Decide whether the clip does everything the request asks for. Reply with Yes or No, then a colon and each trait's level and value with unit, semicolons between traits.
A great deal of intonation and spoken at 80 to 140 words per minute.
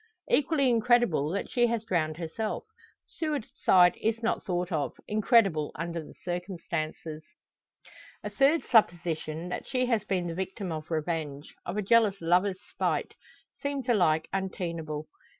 Yes: wide, 5.7 semitones; slow, 135 wpm